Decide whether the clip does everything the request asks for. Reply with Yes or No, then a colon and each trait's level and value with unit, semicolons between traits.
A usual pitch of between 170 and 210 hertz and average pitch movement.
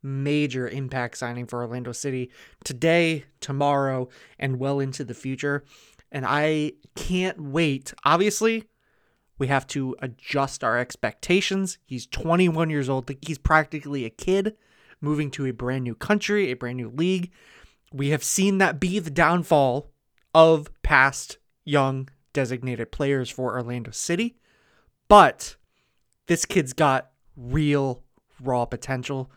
No: medium, 140 Hz; average, 4.0 semitones